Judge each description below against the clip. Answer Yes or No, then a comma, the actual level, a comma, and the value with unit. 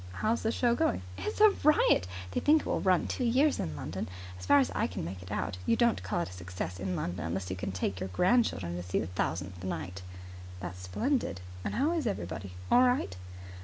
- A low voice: Yes, very low, 95 Hz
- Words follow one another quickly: Yes, fast, 225 wpm